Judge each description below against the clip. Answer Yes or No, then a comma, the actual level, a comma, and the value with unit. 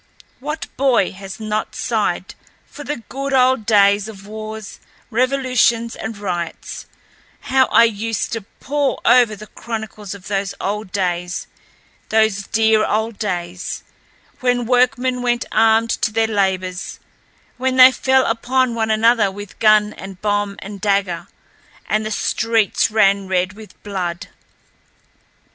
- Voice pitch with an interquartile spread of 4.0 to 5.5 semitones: No, average, 3.2 semitones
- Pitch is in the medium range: No, high, 220 Hz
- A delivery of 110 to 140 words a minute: Yes, slow, 135 wpm